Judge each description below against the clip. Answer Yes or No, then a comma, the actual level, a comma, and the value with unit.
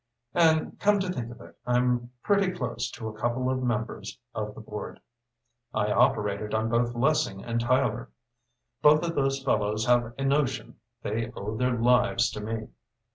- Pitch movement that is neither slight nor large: Yes, average, 3.5 semitones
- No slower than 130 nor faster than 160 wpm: No, average, 170 wpm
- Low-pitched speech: Yes, low, 120 Hz